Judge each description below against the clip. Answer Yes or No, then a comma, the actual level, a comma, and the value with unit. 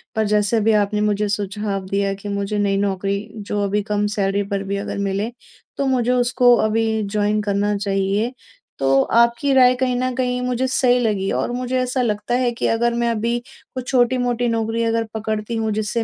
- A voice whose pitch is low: No, high, 220 Hz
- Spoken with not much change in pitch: No, average, 3.1 semitones